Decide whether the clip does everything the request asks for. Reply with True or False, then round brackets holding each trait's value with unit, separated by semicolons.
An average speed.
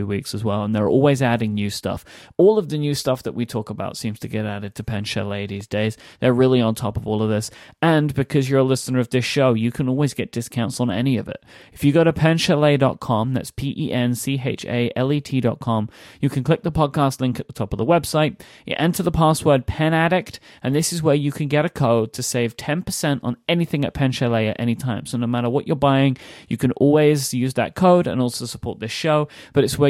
False (230 wpm)